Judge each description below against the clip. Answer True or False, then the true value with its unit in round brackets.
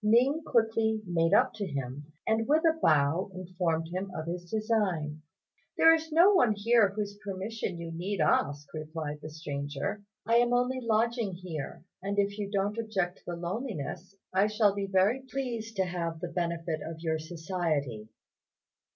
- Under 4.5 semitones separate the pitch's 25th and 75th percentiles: False (5.2 semitones)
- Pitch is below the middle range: False (190 Hz)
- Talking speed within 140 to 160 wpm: False (170 wpm)